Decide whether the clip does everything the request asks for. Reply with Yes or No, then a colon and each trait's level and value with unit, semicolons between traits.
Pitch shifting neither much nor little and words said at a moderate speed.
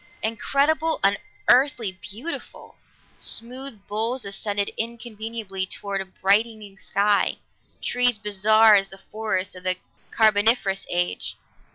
No: average, 3.0 semitones; slow, 100 wpm